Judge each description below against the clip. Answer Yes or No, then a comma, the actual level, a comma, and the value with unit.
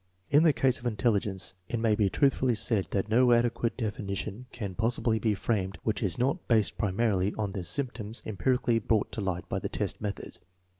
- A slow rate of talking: No, average, 200 wpm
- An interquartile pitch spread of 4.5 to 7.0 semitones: No, average, 3.3 semitones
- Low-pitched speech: Yes, low, 110 Hz